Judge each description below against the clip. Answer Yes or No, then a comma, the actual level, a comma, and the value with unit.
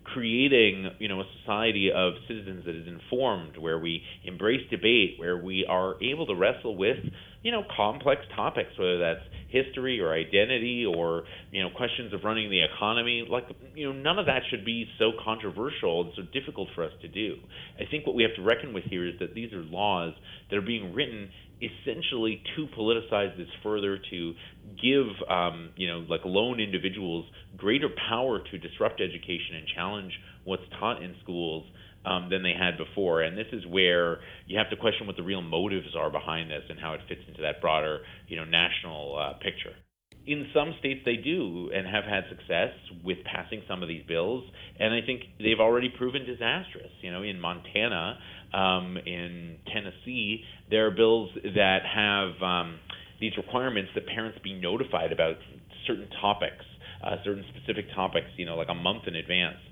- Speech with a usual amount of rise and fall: Yes, average, 4.1 semitones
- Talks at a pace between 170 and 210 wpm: Yes, average, 185 wpm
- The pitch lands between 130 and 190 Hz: No, very low, 95 Hz